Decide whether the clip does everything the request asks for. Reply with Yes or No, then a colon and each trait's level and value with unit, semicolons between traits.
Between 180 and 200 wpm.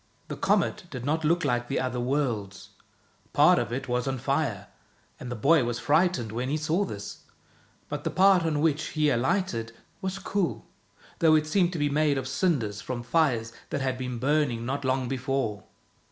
Yes: average, 185 wpm